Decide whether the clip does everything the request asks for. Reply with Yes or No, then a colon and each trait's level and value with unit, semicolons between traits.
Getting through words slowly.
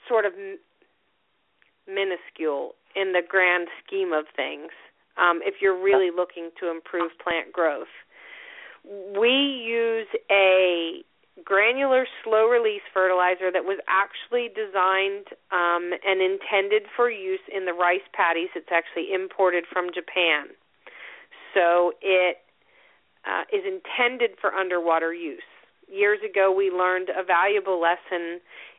Yes: slow, 125 wpm